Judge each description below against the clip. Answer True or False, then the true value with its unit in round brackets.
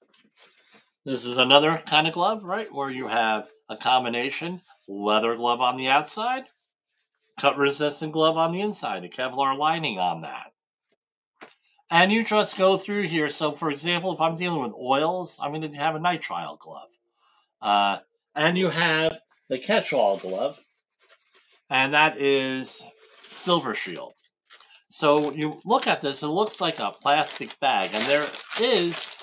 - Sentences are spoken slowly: False (155 wpm)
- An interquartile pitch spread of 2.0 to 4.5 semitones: False (5.1 semitones)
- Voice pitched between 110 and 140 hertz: False (150 Hz)